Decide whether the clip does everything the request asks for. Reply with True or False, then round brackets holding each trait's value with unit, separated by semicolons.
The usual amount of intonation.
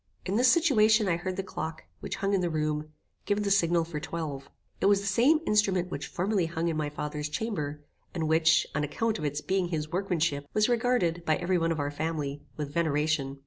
True (4.5 semitones)